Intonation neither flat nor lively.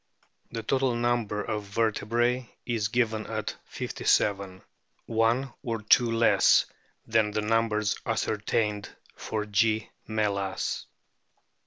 No: narrow, 1.8 semitones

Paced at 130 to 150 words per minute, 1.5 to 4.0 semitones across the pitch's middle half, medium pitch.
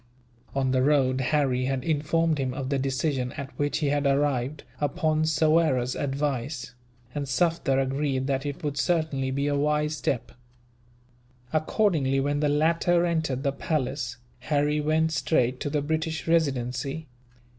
Yes: average, 145 wpm; average, 2.8 semitones; medium, 145 Hz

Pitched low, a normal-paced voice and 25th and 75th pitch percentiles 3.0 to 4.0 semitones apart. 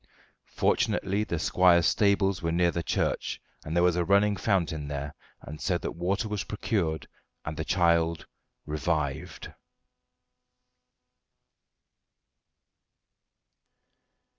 No: very low, 85 Hz; slow, 100 wpm; average, 3.5 semitones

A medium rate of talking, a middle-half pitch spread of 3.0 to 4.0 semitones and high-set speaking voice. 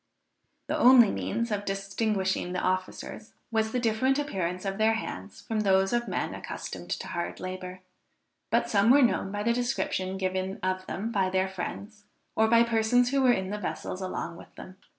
Yes: average, 185 wpm; average, 3.6 semitones; high, 200 Hz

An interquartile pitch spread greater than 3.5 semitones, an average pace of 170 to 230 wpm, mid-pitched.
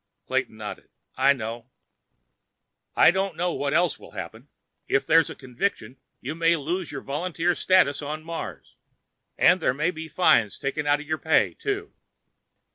No: average, 3.9 semitones; average, 160 wpm; medium, 155 Hz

